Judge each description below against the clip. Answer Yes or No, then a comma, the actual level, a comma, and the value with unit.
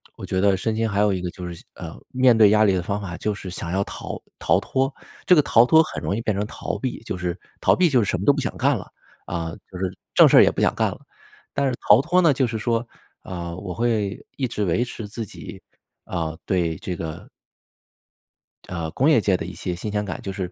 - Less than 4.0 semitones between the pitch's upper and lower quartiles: No, average, 4.7 semitones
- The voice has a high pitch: No, low, 100 Hz